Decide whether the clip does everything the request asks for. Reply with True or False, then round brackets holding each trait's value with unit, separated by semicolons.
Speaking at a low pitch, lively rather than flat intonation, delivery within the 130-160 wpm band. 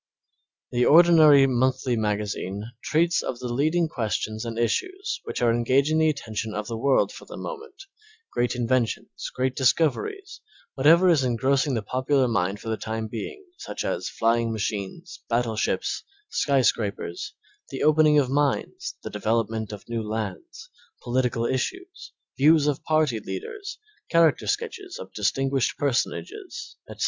True (130 Hz; 5.7 semitones; 145 wpm)